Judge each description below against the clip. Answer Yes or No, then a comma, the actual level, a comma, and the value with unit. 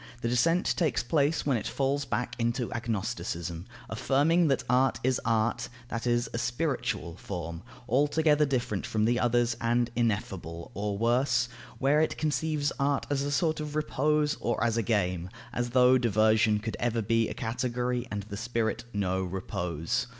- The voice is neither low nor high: No, low, 120 Hz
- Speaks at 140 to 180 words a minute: Yes, average, 165 wpm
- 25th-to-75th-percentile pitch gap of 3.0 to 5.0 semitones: Yes, average, 3.9 semitones